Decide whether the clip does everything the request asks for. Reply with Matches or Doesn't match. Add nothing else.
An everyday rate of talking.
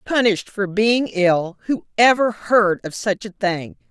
Matches